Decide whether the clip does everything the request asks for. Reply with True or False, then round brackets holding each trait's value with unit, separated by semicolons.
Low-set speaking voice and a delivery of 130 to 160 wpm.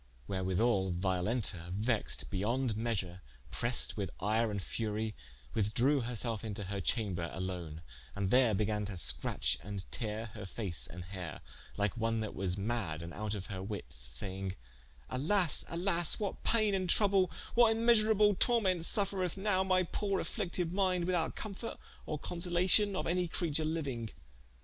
True (115 Hz; 150 wpm)